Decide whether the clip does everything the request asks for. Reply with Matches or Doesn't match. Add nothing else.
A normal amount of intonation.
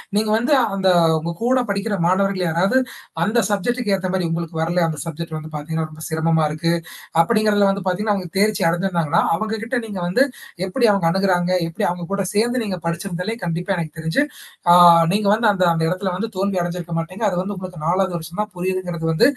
Matches